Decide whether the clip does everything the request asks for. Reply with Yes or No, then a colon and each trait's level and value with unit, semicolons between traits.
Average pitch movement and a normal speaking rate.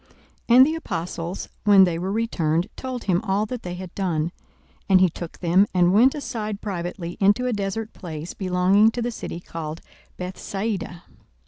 Yes: average, 3.8 semitones; average, 175 wpm